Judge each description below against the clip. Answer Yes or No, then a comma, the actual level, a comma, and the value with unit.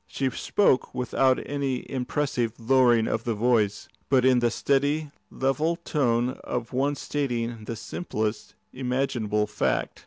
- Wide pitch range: No, average, 2.8 semitones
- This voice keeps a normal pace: No, slow, 130 wpm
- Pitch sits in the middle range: No, low, 125 Hz